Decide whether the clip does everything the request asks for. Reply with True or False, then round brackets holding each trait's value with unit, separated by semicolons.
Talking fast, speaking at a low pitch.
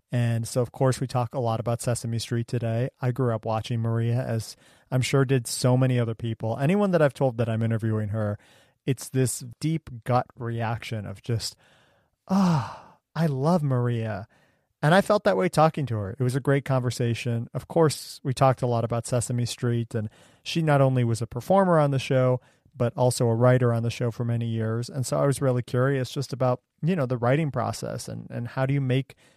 True (215 wpm; 125 Hz)